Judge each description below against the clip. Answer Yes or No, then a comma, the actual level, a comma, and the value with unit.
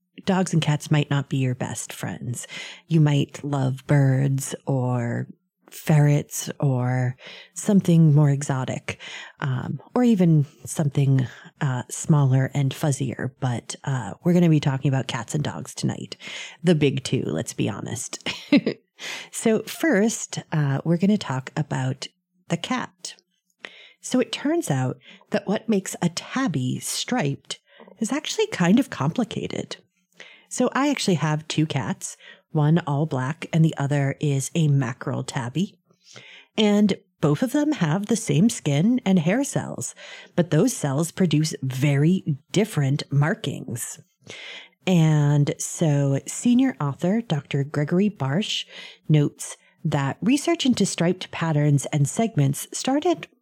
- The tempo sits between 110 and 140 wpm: Yes, slow, 135 wpm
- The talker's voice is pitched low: No, medium, 155 Hz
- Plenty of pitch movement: Yes, wide, 5.7 semitones